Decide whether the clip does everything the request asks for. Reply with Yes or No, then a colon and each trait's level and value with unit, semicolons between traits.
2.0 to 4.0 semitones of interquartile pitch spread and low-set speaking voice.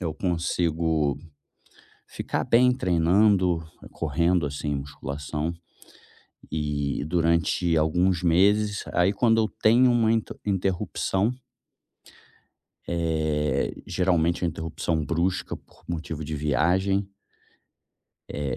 Yes: average, 3.6 semitones; very low, 85 Hz